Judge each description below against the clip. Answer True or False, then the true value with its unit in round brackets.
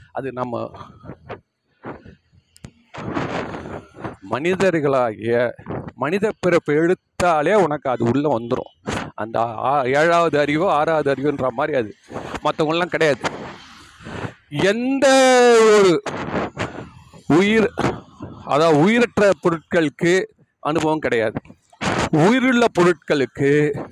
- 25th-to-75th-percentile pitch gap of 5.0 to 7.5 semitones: True (5.4 semitones)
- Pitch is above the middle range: False (165 Hz)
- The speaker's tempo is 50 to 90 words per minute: True (75 wpm)